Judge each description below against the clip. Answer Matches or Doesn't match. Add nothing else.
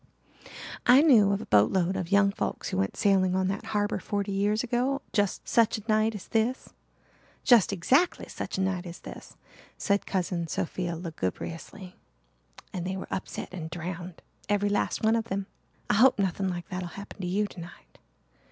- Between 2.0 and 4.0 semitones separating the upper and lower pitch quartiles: Matches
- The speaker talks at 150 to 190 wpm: Matches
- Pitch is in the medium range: Doesn't match